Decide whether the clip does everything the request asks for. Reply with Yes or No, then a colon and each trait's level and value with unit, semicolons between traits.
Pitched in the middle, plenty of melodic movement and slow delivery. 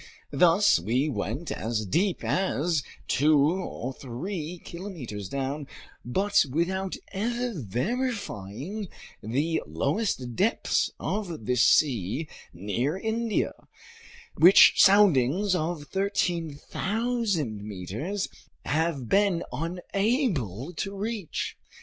Yes: medium, 165 Hz; wide, 7.8 semitones; slow, 90 wpm